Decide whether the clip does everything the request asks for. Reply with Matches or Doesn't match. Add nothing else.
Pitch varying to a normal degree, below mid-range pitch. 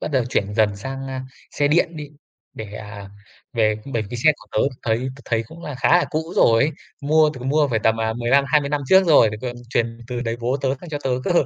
Matches